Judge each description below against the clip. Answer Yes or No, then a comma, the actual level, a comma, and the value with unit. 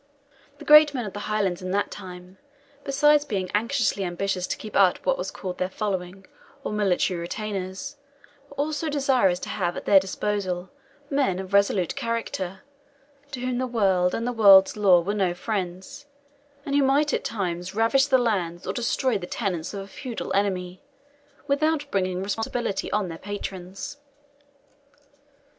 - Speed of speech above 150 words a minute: Yes, average, 160 wpm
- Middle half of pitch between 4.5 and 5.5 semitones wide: Yes, average, 5.1 semitones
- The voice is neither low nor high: No, high, 200 Hz